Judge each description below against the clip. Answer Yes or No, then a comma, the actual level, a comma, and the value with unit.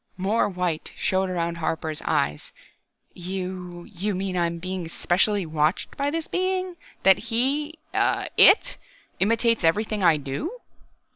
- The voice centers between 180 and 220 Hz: Yes, medium, 185 Hz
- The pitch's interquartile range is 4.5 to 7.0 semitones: Yes, average, 5.2 semitones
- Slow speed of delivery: Yes, slow, 130 wpm